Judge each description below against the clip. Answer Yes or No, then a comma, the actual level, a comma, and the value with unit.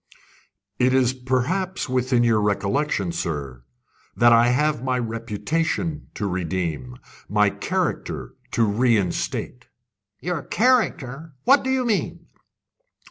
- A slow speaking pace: Yes, slow, 110 wpm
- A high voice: No, low, 125 Hz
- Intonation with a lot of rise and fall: Yes, wide, 6.7 semitones